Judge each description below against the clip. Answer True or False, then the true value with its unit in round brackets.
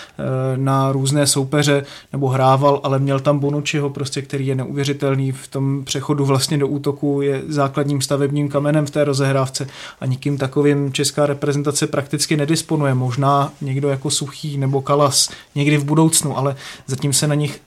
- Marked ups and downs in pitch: False (1.2 semitones)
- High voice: False (140 Hz)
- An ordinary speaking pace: True (160 wpm)